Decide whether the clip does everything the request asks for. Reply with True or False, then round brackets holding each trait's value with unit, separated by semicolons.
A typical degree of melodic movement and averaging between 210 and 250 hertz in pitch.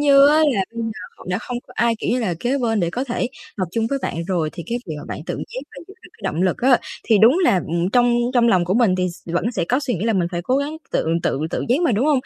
False (5.8 semitones; 230 Hz)